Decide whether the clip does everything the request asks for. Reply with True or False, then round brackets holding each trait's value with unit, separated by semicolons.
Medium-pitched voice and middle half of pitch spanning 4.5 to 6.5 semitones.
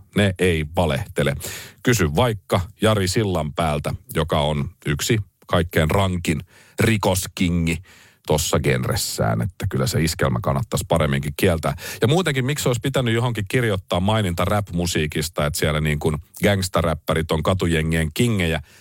False (90 Hz; 5.0 semitones)